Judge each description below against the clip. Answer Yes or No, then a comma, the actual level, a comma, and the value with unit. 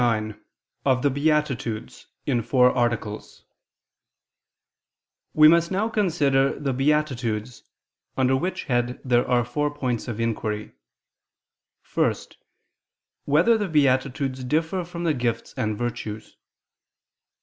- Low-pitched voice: Yes, low, 130 Hz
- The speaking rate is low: Yes, slow, 115 wpm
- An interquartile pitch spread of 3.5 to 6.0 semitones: Yes, average, 4.1 semitones